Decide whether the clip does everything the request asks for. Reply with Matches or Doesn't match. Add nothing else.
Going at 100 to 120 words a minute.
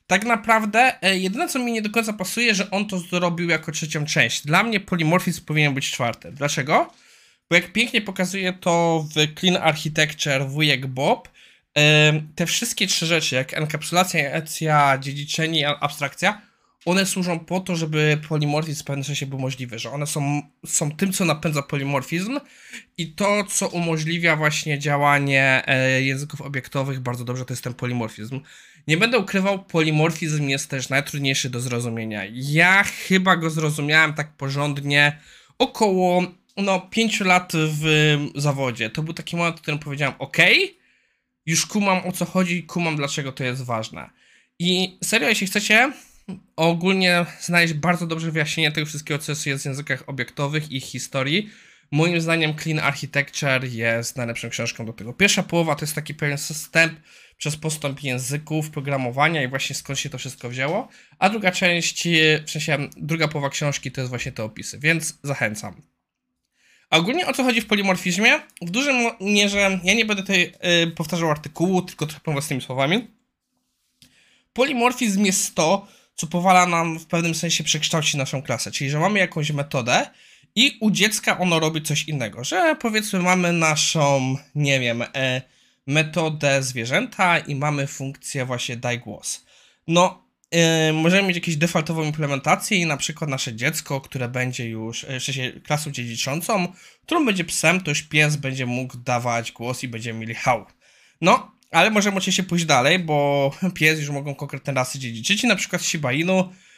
Doesn't match